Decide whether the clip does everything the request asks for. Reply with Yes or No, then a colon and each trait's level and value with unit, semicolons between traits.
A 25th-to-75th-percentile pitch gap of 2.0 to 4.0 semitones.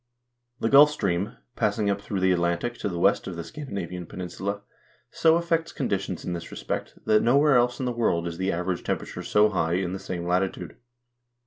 No: average, 5.3 semitones